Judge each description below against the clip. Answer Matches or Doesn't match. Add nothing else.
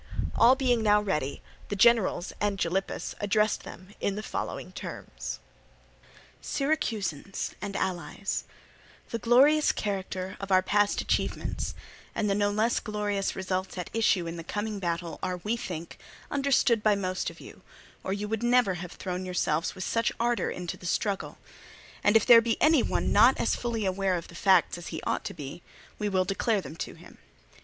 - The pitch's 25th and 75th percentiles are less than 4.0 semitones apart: Matches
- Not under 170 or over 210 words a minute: Matches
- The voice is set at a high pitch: Matches